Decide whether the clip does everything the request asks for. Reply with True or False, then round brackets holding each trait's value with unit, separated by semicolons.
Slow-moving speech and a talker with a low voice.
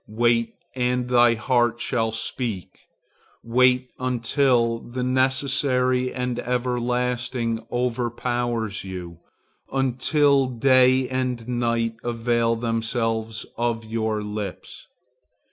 True (90 wpm; 120 Hz)